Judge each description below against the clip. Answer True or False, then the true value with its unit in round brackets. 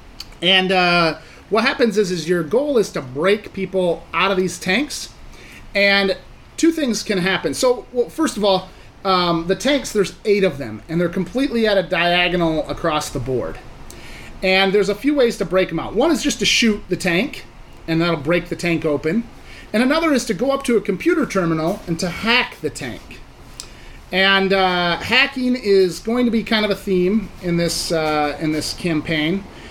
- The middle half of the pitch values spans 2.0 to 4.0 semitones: False (4.6 semitones)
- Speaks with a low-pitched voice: False (190 Hz)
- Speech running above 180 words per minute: True (195 wpm)